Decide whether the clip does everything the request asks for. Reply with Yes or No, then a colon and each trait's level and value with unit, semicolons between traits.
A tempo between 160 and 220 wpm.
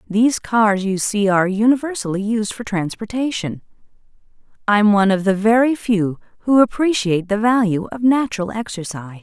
No: average, 150 wpm